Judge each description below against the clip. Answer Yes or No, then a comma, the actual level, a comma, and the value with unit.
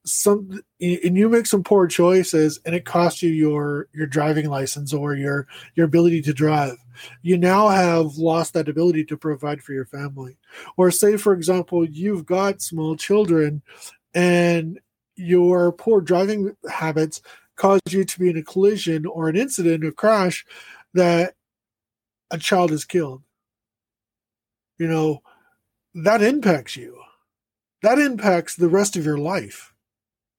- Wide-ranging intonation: No, average, 3.8 semitones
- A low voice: No, medium, 165 Hz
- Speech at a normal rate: Yes, average, 145 wpm